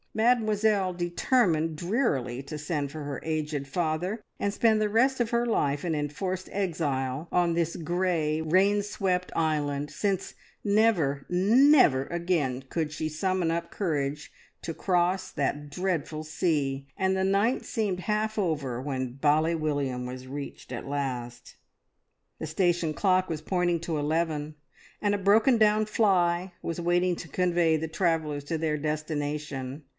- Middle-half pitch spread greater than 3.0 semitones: Yes, average, 4.4 semitones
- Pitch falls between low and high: Yes, medium, 165 Hz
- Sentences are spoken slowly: No, average, 145 wpm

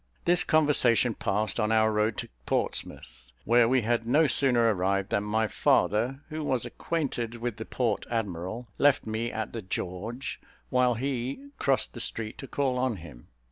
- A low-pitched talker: Yes, low, 115 Hz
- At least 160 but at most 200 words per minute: Yes, average, 170 wpm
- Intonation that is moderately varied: Yes, average, 3.3 semitones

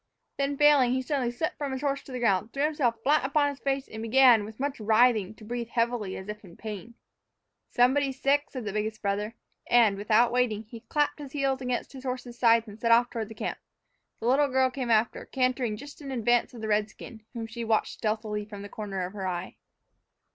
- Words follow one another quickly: Yes, fast, 220 wpm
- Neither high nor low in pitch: No, high, 235 Hz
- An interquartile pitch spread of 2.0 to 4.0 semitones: Yes, average, 3.7 semitones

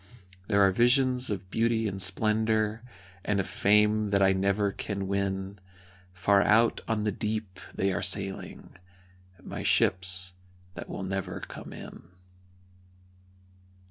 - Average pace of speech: No, slow, 130 wpm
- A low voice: Yes, low, 100 Hz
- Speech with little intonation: Yes, narrow, 2.1 semitones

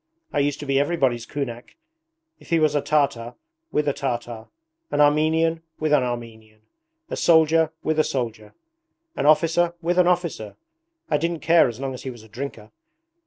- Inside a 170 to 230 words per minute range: Yes, average, 175 wpm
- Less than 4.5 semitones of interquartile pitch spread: No, average, 5.1 semitones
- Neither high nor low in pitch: Yes, medium, 145 Hz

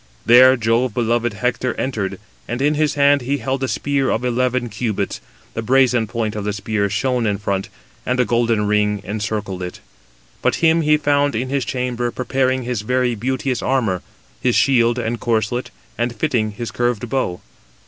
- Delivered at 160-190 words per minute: Yes, average, 175 wpm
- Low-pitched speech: Yes, low, 120 Hz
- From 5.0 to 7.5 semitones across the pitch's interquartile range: No, average, 3.1 semitones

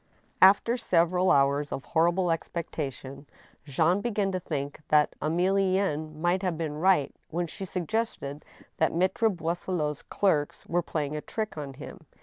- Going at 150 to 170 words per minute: No, average, 140 wpm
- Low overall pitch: No, medium, 170 Hz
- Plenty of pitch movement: No, average, 4.0 semitones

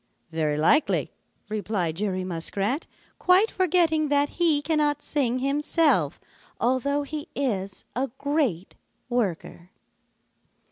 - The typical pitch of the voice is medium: No, very high, 270 Hz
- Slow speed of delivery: Yes, slow, 100 wpm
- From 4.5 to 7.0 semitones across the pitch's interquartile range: No, wide, 7.7 semitones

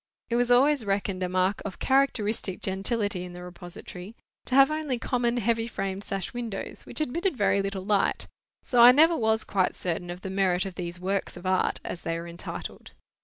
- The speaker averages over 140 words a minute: Yes, average, 195 wpm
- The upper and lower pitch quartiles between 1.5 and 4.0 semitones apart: No, average, 4.7 semitones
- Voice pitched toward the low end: No, high, 200 Hz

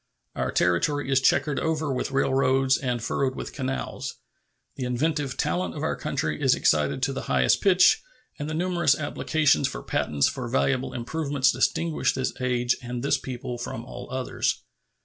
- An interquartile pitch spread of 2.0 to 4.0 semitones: Yes, average, 2.9 semitones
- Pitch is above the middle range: No, low, 130 Hz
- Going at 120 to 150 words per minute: No, average, 165 wpm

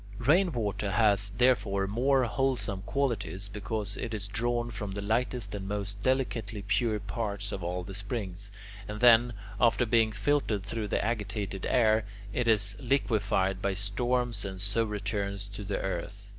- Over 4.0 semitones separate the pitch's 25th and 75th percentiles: No, average, 3.1 semitones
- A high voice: No, low, 105 Hz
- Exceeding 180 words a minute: No, average, 155 wpm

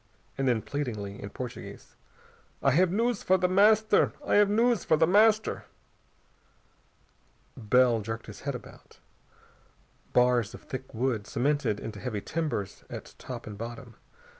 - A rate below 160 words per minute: Yes, average, 140 wpm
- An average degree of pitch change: No, wide, 8.3 semitones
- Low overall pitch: Yes, low, 130 Hz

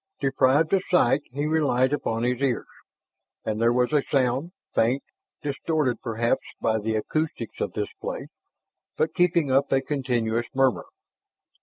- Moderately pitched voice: No, low, 130 Hz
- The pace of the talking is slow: No, average, 145 wpm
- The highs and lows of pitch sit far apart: No, average, 3.7 semitones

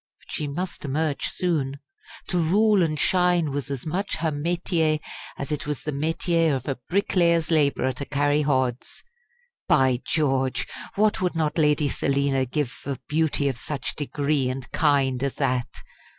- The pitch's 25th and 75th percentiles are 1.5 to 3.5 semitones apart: Yes, average, 3.2 semitones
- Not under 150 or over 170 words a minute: Yes, average, 160 wpm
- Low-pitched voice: No, medium, 150 Hz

